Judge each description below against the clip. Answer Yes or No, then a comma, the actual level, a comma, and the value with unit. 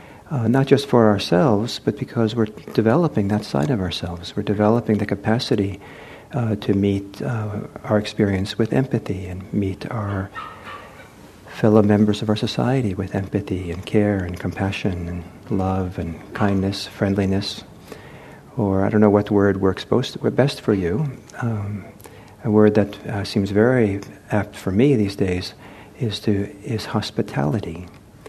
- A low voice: Yes, low, 105 Hz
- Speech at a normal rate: Yes, average, 150 wpm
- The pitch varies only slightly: Yes, narrow, 2.3 semitones